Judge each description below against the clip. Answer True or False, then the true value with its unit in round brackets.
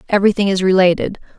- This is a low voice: False (190 Hz)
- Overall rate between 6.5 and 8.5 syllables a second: True (7.6 syllables/s)